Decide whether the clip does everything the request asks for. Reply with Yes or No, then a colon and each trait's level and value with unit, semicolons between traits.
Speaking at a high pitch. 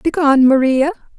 Yes: very high, 280 Hz